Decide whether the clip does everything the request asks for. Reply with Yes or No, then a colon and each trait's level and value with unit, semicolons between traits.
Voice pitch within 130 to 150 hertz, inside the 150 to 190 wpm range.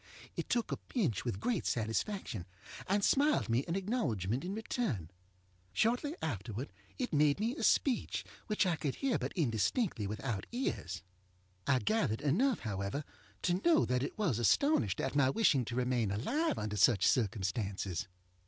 Yes: medium, 140 Hz; average, 155 wpm